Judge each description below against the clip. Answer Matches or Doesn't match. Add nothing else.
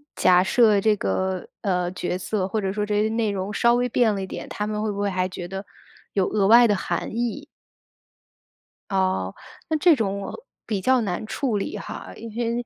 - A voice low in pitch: Doesn't match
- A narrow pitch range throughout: Doesn't match